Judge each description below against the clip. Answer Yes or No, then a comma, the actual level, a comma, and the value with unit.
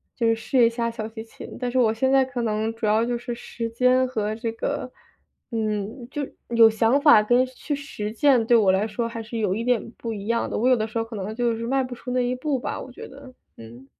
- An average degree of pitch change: No, narrow, 2.3 semitones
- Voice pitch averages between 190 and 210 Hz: No, high, 230 Hz